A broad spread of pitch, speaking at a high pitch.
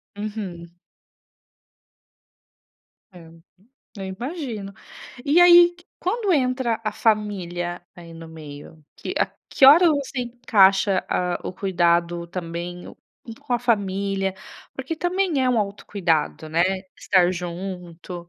Yes: wide, 6.4 semitones; high, 195 Hz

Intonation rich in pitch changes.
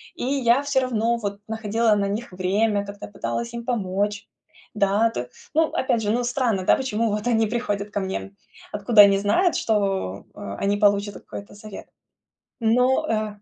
No: average, 2.7 semitones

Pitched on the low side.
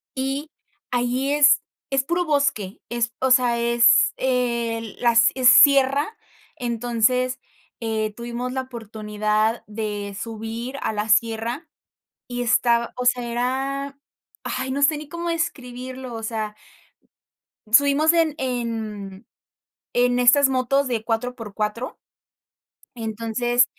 No: high, 245 Hz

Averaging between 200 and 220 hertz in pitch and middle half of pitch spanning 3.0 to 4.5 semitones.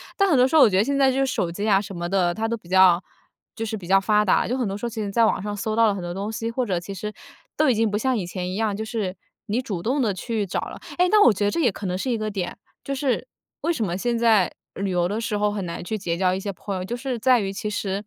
Yes: high, 210 Hz; average, 3.6 semitones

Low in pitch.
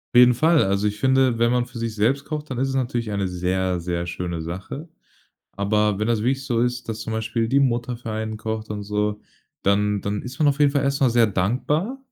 Yes: low, 115 Hz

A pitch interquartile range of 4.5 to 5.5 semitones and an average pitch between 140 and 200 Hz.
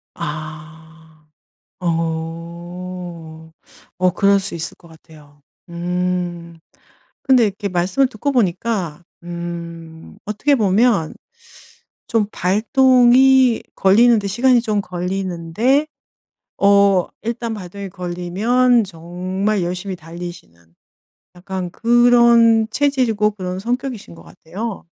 Yes: average, 5.1 semitones; medium, 185 Hz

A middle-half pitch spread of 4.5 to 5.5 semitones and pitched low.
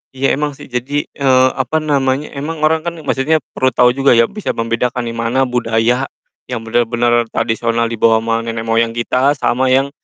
No: average, 2.9 semitones; low, 125 Hz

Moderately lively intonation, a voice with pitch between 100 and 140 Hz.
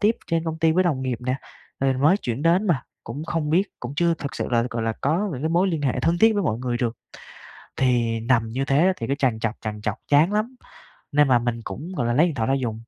No: wide, 5.7 semitones; low, 135 Hz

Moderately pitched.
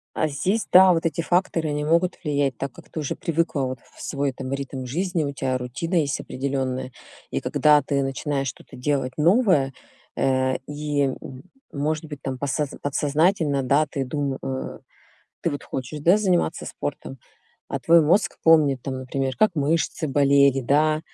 Yes: medium, 145 Hz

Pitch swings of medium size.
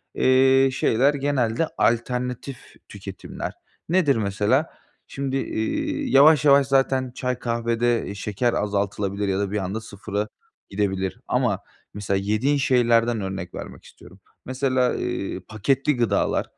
Yes: average, 4.6 semitones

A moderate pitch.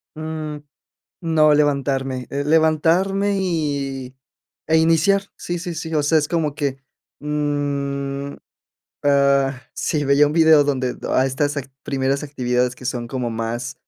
Yes: medium, 145 Hz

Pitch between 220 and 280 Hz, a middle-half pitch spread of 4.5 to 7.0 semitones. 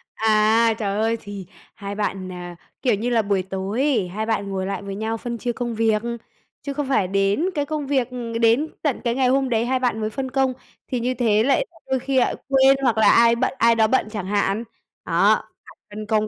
No: high, 225 Hz; average, 3.8 semitones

